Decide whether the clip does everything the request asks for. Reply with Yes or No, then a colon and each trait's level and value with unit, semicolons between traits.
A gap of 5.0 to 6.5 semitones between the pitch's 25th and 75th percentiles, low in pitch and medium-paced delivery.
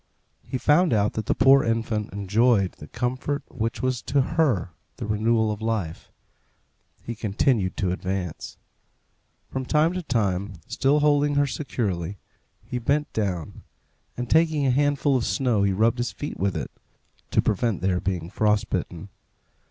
Yes: average, 5.3 semitones; low, 115 Hz; average, 155 wpm